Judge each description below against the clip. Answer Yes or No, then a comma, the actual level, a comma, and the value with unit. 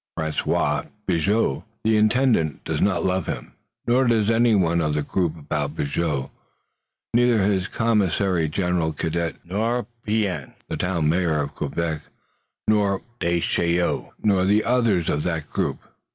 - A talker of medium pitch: No, very low, 90 Hz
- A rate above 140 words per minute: No, slow, 135 wpm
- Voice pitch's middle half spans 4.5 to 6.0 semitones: Yes, average, 4.9 semitones